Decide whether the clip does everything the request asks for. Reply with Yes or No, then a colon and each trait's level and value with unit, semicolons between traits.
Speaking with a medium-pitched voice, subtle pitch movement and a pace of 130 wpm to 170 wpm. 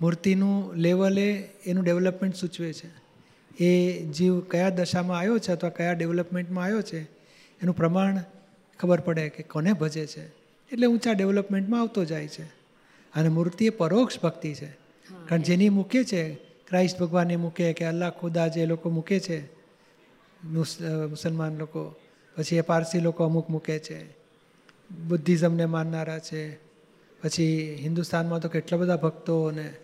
Yes: medium, 170 Hz; narrow, 2.2 semitones; fast, 140 wpm